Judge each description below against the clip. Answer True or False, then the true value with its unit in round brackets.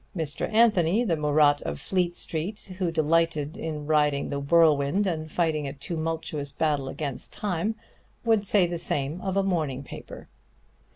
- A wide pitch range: False (3.6 semitones)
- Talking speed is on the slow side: False (155 wpm)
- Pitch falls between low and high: True (160 Hz)